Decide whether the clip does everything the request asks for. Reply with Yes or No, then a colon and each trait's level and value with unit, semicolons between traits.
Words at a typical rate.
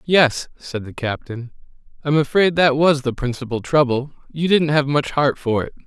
Yes: average, 175 wpm